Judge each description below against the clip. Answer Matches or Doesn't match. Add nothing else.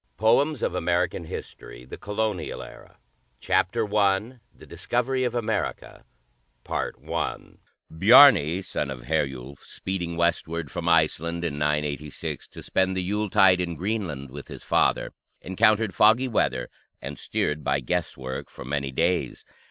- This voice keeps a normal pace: Doesn't match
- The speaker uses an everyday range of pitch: Doesn't match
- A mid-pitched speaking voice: Doesn't match